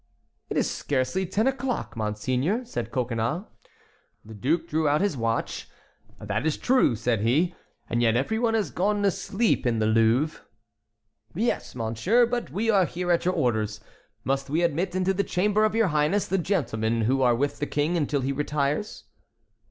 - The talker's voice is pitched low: No, medium, 150 Hz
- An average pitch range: No, wide, 8.2 semitones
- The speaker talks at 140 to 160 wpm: No, average, 175 wpm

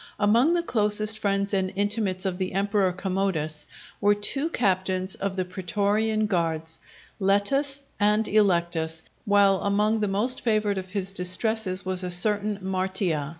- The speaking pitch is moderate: No, high, 200 Hz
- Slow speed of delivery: No, average, 145 wpm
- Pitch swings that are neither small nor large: No, narrow, 2.3 semitones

